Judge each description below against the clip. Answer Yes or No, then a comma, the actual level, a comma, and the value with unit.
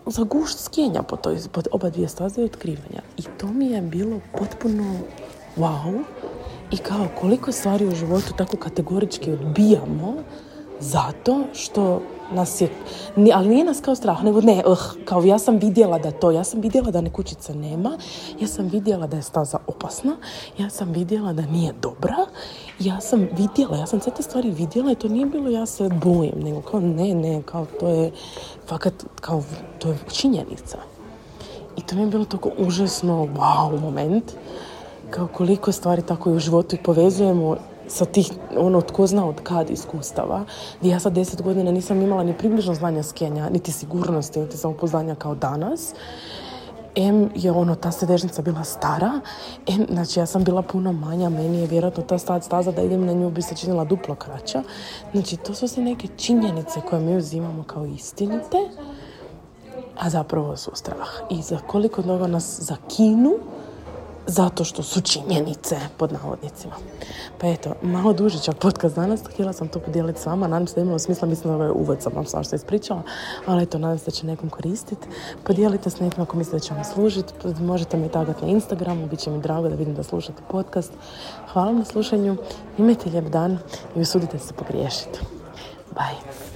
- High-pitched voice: No, medium, 180 Hz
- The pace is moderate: No, fast, 180 wpm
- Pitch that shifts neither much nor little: Yes, average, 3.8 semitones